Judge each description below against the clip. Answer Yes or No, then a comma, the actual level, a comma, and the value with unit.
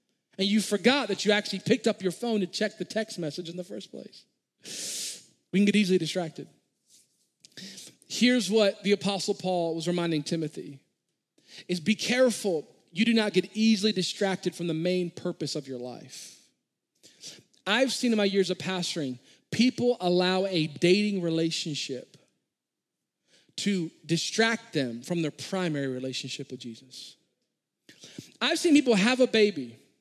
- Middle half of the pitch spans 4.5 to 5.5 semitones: Yes, average, 4.8 semitones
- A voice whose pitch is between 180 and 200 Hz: Yes, medium, 185 Hz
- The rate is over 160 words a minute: No, average, 150 wpm